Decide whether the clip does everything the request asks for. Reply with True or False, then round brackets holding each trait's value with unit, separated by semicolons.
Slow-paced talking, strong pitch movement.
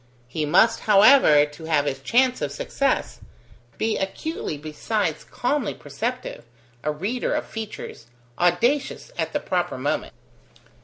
True (125 wpm; 8.7 semitones)